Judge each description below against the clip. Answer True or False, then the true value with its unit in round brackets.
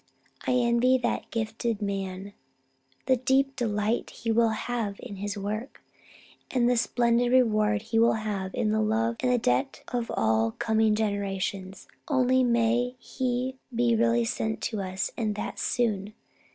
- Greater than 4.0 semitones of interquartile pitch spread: False (2.8 semitones)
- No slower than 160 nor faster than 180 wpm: False (150 wpm)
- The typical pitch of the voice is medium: False (225 Hz)